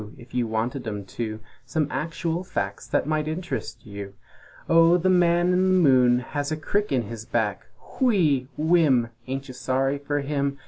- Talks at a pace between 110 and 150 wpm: No, average, 175 wpm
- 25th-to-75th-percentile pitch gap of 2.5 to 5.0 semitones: No, wide, 5.6 semitones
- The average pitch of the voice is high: No, medium, 140 Hz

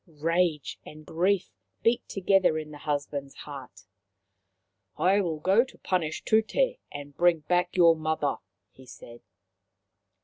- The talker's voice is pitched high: No, medium, 160 Hz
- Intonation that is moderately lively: Yes, average, 4.1 semitones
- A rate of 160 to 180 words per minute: No, slow, 135 wpm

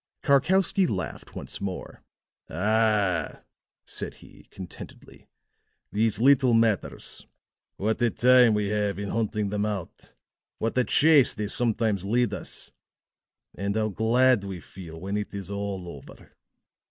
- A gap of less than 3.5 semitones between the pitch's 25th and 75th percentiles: Yes, average, 3.1 semitones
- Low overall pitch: Yes, low, 105 Hz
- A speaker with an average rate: No, slow, 130 wpm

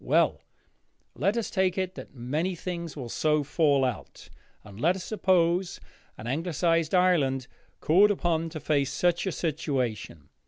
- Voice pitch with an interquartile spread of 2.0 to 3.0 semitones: No, average, 4.6 semitones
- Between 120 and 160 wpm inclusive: Yes, average, 145 wpm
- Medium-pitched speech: Yes, medium, 165 Hz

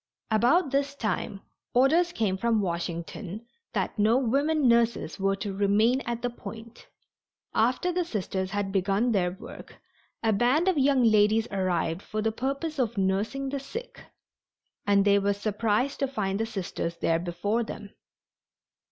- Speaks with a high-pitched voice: Yes, high, 220 Hz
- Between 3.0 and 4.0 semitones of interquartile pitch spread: No, average, 4.9 semitones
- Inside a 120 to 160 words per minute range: Yes, average, 150 wpm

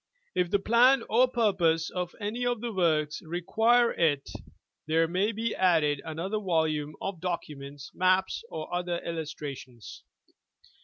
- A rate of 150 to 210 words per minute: No, slow, 135 wpm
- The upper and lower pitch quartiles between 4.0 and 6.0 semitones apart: Yes, average, 5.1 semitones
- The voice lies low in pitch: No, medium, 175 Hz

